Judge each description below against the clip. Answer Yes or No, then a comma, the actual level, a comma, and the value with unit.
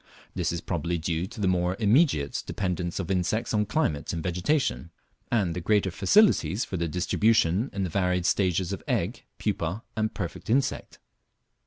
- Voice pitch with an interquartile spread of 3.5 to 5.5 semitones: Yes, average, 3.9 semitones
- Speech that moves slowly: No, average, 165 wpm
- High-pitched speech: No, very low, 90 Hz